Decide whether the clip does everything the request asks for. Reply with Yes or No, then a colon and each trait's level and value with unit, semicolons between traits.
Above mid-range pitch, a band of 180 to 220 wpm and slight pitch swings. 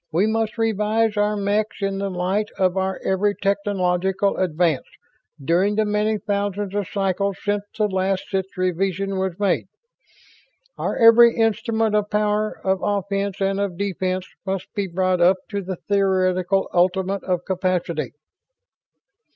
No: high, 195 Hz; average, 145 wpm; narrow, 1.9 semitones